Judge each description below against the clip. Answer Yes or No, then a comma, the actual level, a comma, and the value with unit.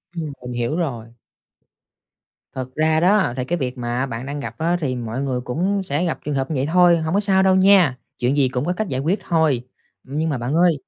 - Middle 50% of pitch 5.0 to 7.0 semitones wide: Yes, wide, 5.4 semitones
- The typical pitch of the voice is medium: Yes, medium, 145 Hz